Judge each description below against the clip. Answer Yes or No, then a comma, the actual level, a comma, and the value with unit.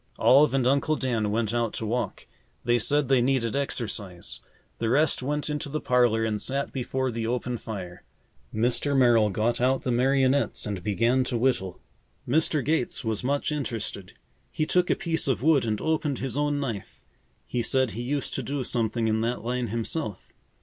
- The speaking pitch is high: No, low, 125 Hz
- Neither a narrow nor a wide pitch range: Yes, average, 3.7 semitones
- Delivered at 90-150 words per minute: No, average, 180 wpm